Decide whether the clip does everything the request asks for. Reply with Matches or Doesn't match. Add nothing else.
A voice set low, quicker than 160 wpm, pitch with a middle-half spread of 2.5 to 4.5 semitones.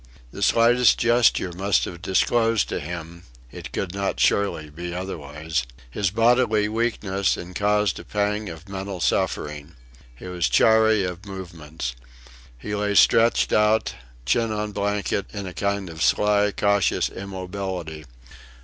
Doesn't match